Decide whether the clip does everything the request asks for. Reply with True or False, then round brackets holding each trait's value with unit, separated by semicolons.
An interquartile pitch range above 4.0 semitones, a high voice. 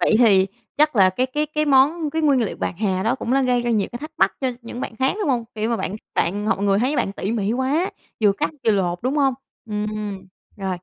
True (5.1 semitones; 230 Hz)